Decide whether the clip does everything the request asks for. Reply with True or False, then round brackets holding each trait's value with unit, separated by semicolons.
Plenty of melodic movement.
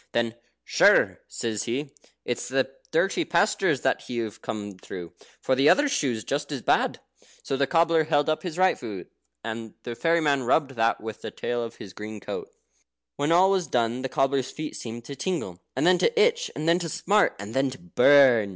True (6.3 semitones)